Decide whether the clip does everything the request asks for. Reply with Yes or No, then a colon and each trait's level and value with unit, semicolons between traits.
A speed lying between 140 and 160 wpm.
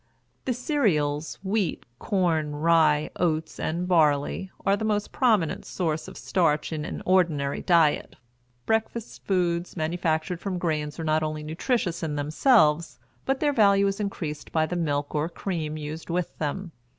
Yes: average, 150 wpm